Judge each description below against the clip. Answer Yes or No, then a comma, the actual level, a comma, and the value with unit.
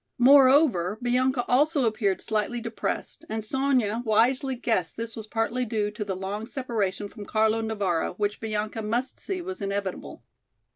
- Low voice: No, high, 225 Hz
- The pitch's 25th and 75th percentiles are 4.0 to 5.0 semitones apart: No, average, 3.4 semitones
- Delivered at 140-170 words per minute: Yes, average, 150 wpm